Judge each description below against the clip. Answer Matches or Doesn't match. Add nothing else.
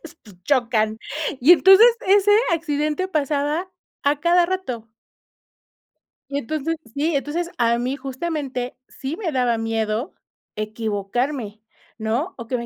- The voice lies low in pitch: Doesn't match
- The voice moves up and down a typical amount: Doesn't match